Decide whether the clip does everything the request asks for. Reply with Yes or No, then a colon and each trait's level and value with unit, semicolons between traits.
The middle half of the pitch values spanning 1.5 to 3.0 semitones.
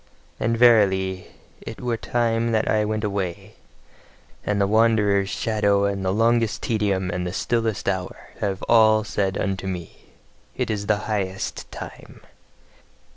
Yes: average, 2.7 semitones